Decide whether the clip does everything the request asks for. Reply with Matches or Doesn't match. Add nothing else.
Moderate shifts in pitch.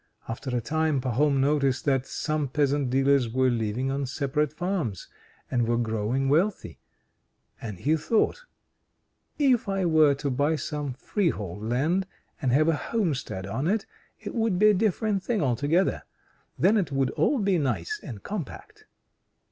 Doesn't match